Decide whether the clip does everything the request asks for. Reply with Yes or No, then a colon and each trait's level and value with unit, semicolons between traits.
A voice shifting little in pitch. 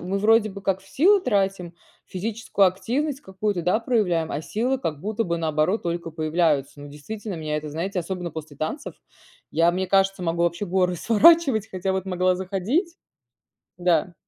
No: average, 4.1 semitones